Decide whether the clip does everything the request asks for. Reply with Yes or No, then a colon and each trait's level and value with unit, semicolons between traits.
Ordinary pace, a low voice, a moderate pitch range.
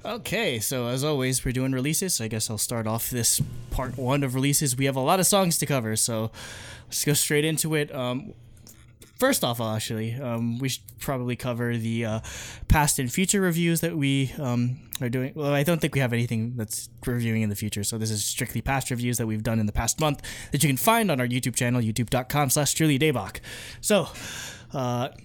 No: fast, 215 wpm; low, 125 Hz; average, 3.6 semitones